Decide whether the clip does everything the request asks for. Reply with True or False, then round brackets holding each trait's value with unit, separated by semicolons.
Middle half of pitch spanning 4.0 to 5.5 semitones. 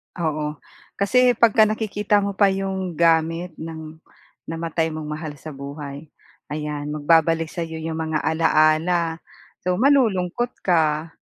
False (3.5 semitones)